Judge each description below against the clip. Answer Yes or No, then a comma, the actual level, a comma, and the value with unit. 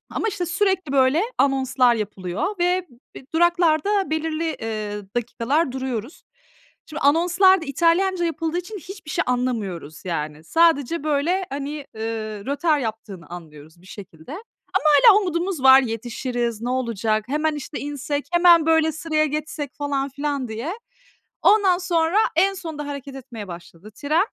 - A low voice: No, very high, 285 Hz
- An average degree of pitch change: No, wide, 6.6 semitones